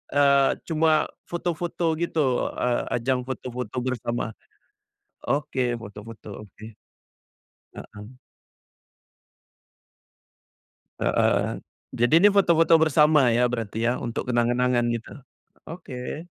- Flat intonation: No, average, 4.7 semitones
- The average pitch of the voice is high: No, low, 125 Hz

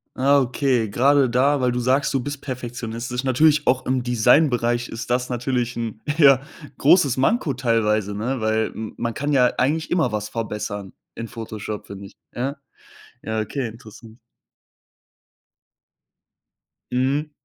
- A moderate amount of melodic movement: Yes, average, 3.1 semitones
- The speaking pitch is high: No, low, 125 Hz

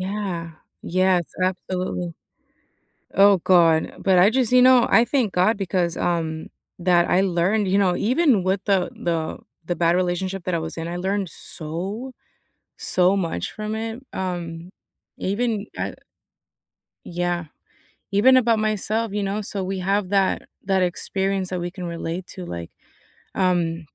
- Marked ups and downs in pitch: No, average, 2.8 semitones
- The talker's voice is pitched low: No, medium, 185 Hz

